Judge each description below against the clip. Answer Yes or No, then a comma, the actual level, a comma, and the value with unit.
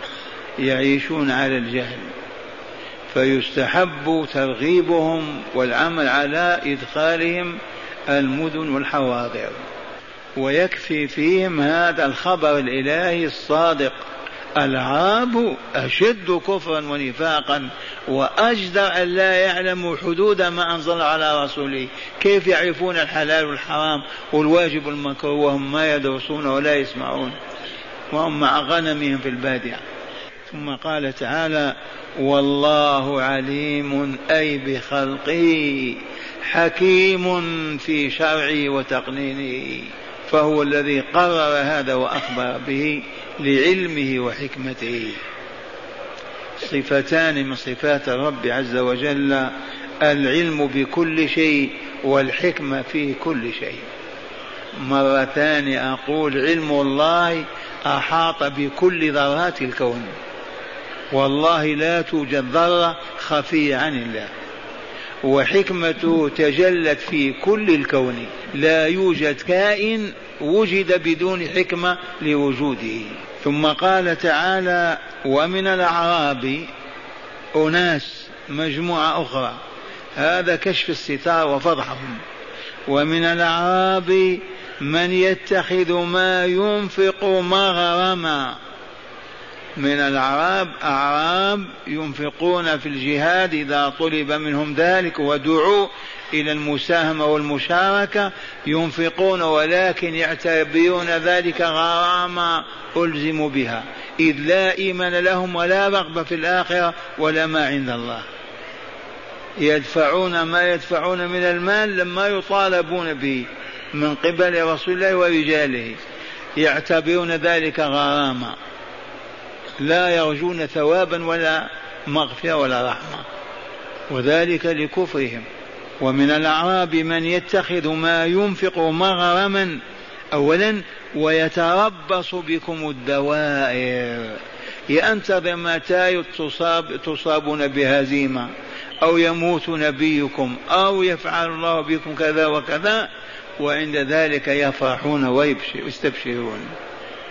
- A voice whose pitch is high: No, medium, 155 Hz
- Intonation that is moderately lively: Yes, average, 3.7 semitones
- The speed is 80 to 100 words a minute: Yes, average, 85 wpm